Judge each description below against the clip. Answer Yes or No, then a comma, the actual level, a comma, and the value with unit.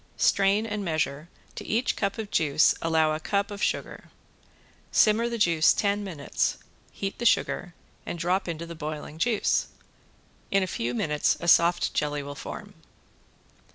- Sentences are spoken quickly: No, average, 155 wpm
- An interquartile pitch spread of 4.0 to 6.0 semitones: Yes, average, 4.5 semitones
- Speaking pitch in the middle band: Yes, medium, 170 Hz